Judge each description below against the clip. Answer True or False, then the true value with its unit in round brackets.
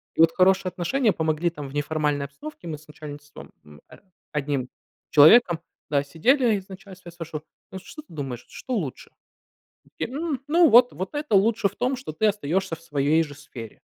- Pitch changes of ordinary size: False (6.8 semitones)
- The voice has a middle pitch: True (165 Hz)